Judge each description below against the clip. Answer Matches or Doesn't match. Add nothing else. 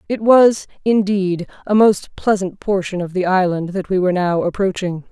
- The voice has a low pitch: Doesn't match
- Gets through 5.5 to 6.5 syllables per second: Doesn't match